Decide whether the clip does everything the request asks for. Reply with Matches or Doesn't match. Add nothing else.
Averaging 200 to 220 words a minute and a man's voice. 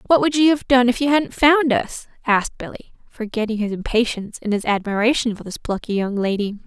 Doesn't match